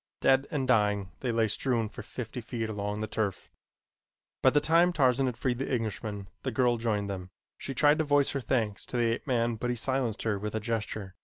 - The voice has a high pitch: No, low, 115 Hz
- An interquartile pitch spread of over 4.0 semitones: No, average, 3.7 semitones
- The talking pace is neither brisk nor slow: No, fast, 220 wpm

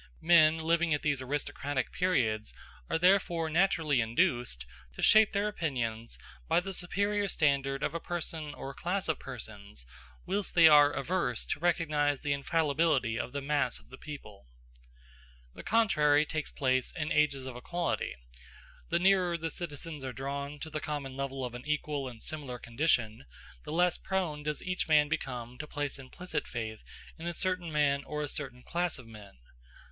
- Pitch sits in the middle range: Yes, medium, 150 Hz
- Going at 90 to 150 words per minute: No, average, 170 wpm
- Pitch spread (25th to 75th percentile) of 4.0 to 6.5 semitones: Yes, average, 4.4 semitones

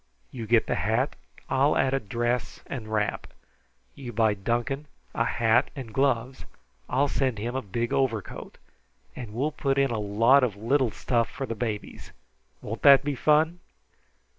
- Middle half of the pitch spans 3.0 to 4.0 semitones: Yes, average, 3.3 semitones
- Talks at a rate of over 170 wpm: No, average, 165 wpm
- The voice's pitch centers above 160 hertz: No, low, 120 Hz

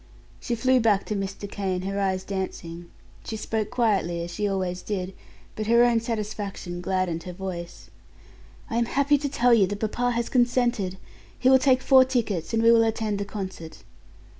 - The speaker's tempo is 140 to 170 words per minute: No, average, 185 wpm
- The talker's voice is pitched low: No, high, 210 Hz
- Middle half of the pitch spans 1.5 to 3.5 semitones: No, average, 3.9 semitones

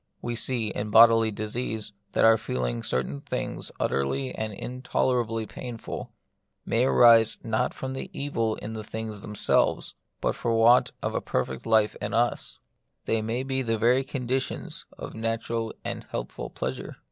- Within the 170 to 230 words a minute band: No, average, 155 wpm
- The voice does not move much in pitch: Yes, narrow, 2.1 semitones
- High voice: No, low, 115 Hz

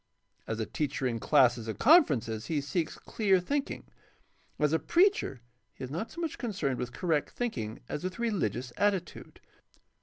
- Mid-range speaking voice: Yes, medium, 155 Hz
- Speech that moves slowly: No, average, 170 wpm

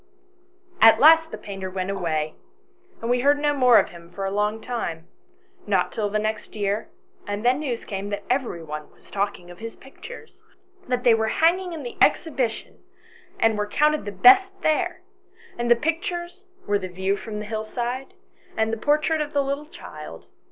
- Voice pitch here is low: No, high, 225 Hz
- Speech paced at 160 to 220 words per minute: Yes, average, 185 wpm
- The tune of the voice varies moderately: No, wide, 6.5 semitones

